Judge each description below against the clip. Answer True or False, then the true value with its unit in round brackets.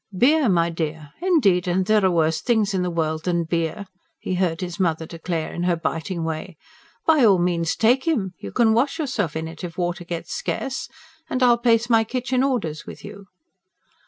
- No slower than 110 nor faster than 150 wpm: False (195 wpm)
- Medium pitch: True (180 Hz)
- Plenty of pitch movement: True (5.9 semitones)